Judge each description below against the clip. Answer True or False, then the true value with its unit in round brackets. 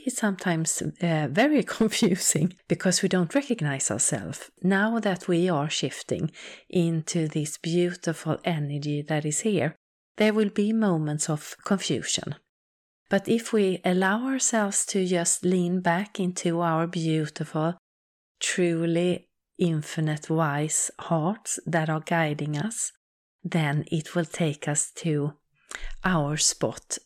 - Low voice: False (170 Hz)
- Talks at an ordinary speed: False (125 wpm)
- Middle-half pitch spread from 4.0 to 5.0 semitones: False (3.6 semitones)